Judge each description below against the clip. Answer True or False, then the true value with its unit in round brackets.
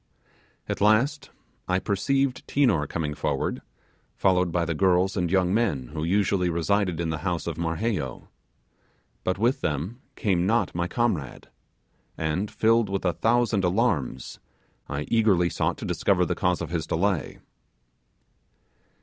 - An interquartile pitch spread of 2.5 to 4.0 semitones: False (4.6 semitones)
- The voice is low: True (90 Hz)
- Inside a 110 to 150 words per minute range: True (140 wpm)